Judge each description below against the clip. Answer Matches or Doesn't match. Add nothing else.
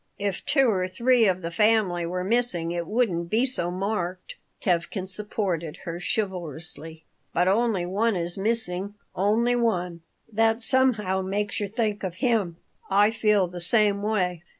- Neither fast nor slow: Matches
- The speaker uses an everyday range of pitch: Matches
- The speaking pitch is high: Matches